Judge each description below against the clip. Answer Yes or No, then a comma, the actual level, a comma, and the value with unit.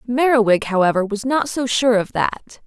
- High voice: Yes, high, 235 Hz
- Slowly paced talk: No, average, 180 wpm